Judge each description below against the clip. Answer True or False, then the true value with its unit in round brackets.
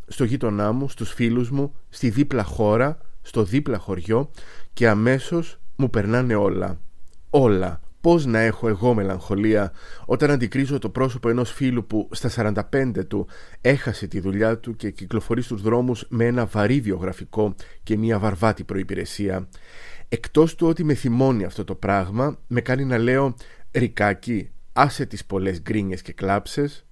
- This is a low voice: True (115 Hz)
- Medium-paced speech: True (150 wpm)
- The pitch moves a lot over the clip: False (4.2 semitones)